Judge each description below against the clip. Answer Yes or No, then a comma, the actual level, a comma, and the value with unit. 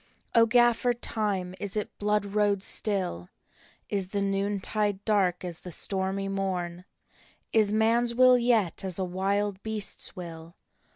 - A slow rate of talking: No, average, 155 wpm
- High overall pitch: Yes, high, 200 Hz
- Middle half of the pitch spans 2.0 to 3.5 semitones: Yes, narrow, 2.4 semitones